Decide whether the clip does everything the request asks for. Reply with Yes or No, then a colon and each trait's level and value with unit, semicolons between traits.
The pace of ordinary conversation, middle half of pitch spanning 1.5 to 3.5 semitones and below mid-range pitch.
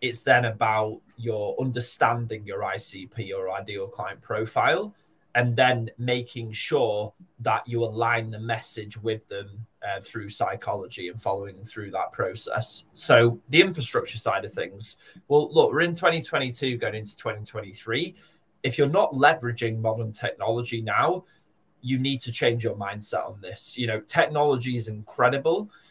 Yes: average, 150 wpm; average, 2.8 semitones; low, 115 Hz